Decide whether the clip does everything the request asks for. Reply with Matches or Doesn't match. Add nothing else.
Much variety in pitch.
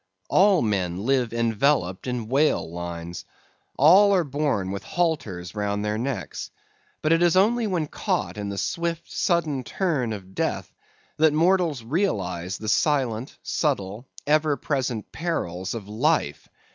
Matches